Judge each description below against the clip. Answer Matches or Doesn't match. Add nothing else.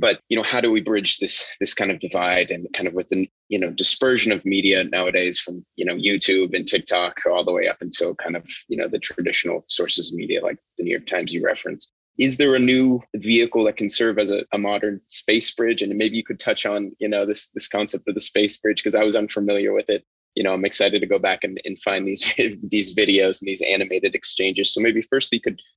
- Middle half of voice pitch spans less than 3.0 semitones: Matches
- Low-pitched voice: Matches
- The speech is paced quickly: Matches